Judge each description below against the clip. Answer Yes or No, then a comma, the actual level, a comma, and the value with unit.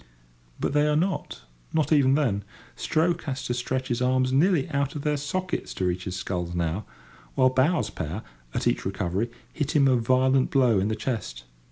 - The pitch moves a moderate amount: No, wide, 7.1 semitones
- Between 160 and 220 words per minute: Yes, average, 185 wpm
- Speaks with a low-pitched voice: Yes, low, 130 Hz